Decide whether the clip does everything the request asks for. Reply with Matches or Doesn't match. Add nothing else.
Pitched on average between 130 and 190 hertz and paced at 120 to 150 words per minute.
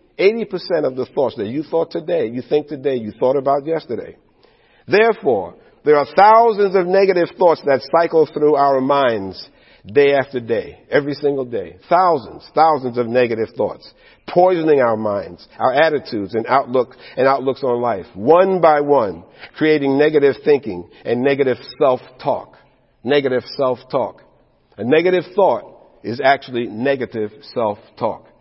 Matches